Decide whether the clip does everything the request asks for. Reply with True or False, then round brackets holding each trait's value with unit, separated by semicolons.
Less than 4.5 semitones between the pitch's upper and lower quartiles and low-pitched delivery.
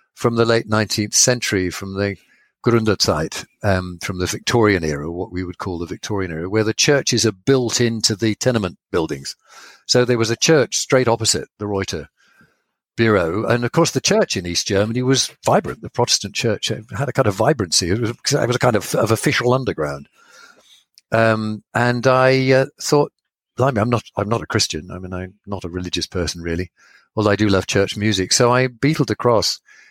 False (4.8 semitones; 110 Hz)